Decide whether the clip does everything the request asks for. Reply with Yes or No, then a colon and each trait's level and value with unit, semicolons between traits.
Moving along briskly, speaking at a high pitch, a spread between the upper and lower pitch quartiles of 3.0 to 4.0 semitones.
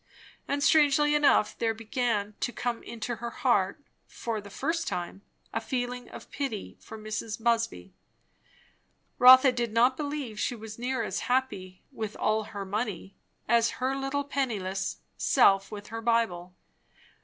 No: average, 145 wpm; high, 230 Hz; average, 3.7 semitones